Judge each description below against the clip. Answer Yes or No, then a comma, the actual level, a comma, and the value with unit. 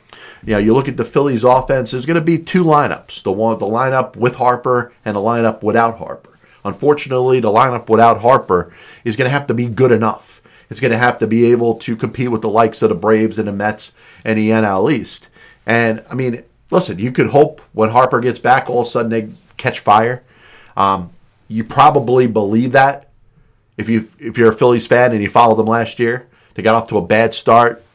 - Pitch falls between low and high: No, low, 115 Hz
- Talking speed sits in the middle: No, fast, 225 wpm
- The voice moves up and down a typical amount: No, narrow, 2.3 semitones